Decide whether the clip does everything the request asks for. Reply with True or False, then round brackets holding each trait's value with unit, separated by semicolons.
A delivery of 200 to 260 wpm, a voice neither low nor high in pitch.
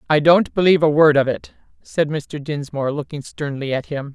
True (205 wpm; 150 Hz)